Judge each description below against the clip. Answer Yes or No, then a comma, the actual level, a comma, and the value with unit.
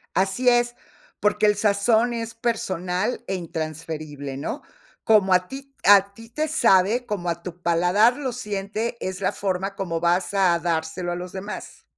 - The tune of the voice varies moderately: Yes, average, 4.4 semitones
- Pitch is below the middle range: No, high, 195 Hz